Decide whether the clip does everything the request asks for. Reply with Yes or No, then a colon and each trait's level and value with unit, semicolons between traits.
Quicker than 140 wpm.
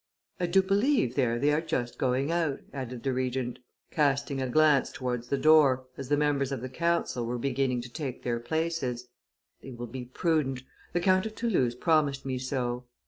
Yes: average, 190 wpm